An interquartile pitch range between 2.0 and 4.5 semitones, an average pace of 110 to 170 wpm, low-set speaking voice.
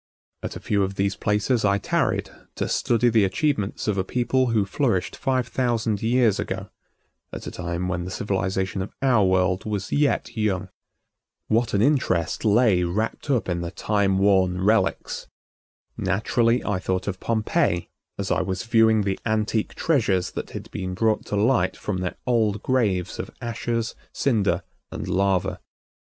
Yes: average, 3.5 semitones; average, 165 wpm; low, 105 Hz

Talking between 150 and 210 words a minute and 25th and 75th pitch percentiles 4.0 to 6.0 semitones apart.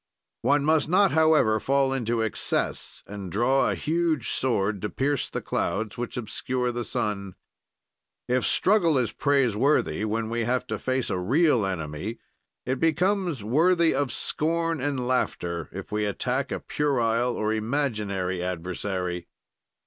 No: average, 140 wpm; wide, 5.6 semitones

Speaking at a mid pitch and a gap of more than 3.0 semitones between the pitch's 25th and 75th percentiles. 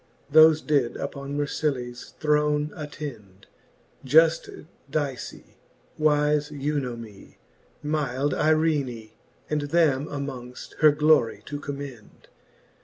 No: medium, 145 Hz; average, 2.7 semitones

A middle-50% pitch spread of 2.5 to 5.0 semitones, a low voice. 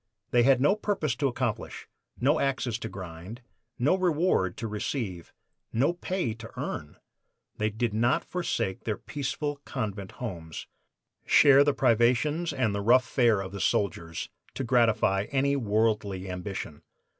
No: wide, 5.4 semitones; low, 115 Hz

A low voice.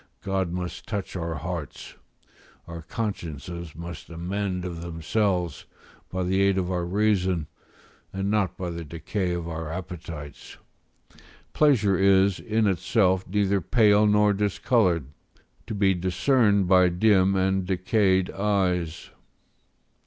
Yes: very low, 95 Hz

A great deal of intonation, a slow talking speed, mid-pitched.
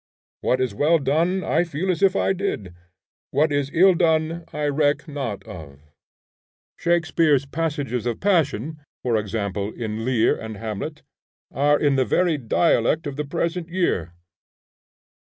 No: wide, 6.3 semitones; average, 145 wpm; medium, 145 Hz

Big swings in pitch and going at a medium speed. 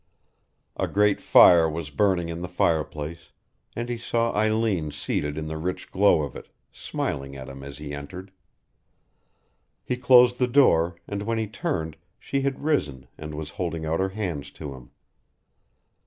Yes: wide, 6.3 semitones; average, 165 wpm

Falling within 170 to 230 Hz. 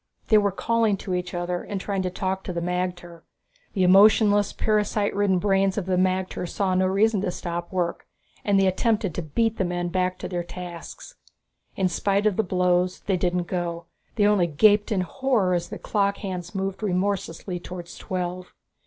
Yes: medium, 185 Hz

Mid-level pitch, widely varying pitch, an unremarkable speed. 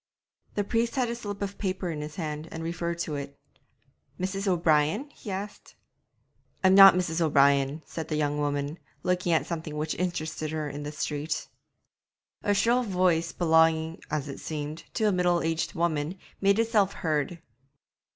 No: medium, 165 Hz; average, 4.0 semitones; average, 165 wpm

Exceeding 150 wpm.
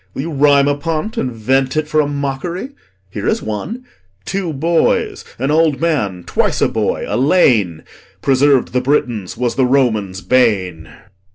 Yes: average, 160 wpm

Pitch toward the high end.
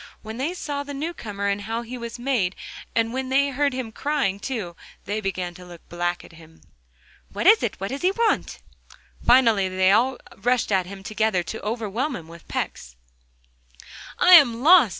Yes: high, 225 Hz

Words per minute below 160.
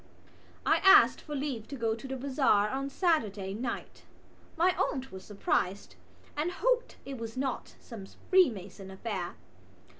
Yes: average, 145 wpm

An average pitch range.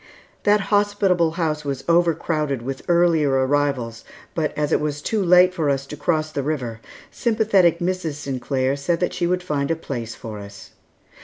Yes: average, 4.3 semitones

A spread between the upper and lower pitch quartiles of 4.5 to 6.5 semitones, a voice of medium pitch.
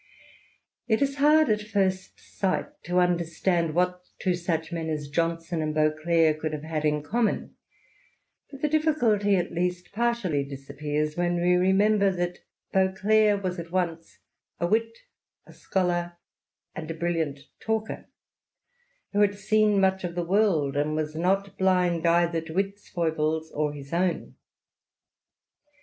No: average, 3.7 semitones; medium, 175 Hz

